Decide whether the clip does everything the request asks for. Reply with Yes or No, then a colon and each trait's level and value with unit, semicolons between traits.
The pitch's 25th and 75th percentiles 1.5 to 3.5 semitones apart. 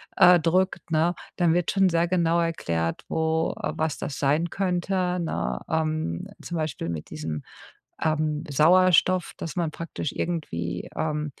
Yes: narrow, 2.6 semitones